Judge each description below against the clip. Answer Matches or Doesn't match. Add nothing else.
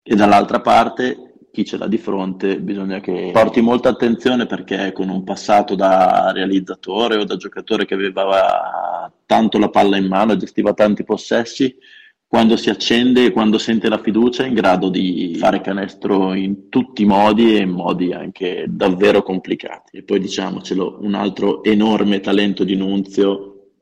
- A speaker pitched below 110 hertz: Matches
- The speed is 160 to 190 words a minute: Matches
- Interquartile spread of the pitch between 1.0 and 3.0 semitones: Matches